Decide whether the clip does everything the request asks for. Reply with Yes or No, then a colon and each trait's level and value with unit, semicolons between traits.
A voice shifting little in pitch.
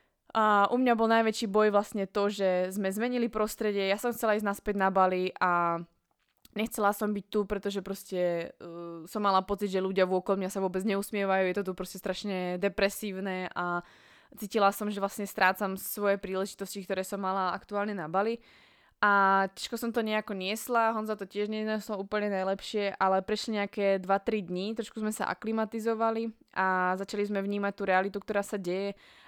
Yes: narrow, 2.0 semitones